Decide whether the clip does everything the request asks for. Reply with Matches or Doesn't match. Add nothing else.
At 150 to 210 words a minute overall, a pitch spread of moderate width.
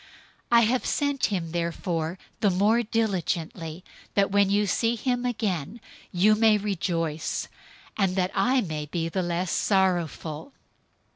Doesn't match